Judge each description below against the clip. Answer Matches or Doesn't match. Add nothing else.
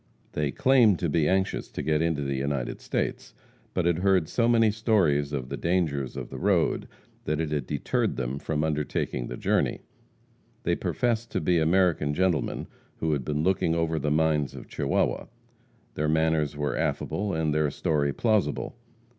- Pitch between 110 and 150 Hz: Doesn't match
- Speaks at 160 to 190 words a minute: Matches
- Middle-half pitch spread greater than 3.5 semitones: Matches